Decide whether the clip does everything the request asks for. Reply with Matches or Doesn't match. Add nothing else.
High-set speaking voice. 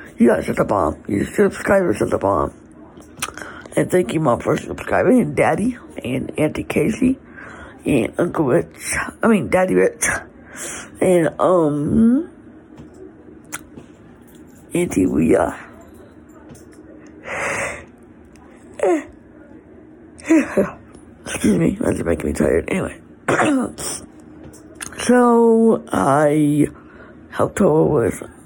Matches